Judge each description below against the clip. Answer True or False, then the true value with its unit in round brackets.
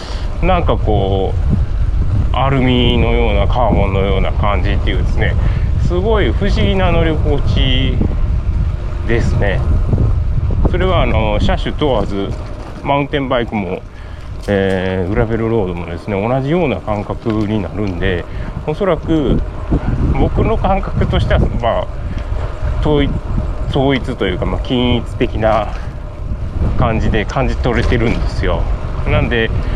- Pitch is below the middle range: True (100 Hz)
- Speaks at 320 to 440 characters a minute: False (265 characters per minute)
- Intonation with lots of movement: False (3.9 semitones)